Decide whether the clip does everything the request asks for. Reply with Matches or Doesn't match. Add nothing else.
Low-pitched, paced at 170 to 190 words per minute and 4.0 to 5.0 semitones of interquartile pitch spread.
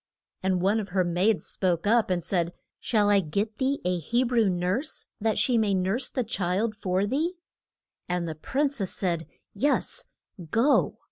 Doesn't match